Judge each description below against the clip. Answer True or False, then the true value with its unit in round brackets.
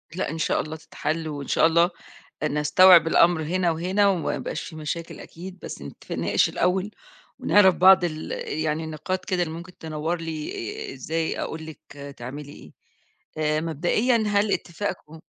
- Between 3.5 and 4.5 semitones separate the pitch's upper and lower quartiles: False (3.0 semitones)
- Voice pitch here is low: False (165 Hz)